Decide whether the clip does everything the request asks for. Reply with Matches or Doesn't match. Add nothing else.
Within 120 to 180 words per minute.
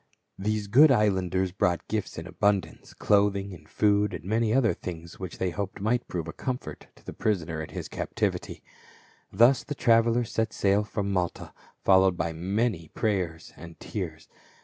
Matches